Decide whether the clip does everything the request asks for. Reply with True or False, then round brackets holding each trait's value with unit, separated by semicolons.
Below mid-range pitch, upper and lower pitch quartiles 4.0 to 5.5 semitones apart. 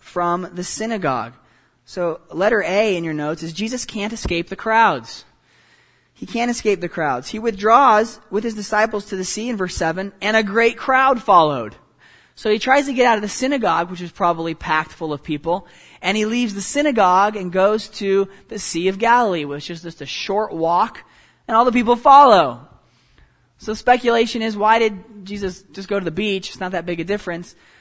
False (205 Hz; 4.3 semitones)